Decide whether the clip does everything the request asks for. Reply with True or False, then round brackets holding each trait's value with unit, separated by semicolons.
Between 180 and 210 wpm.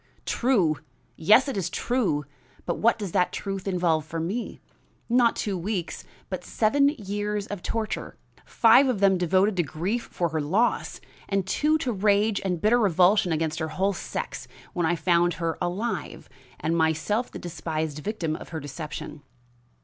False (165 wpm)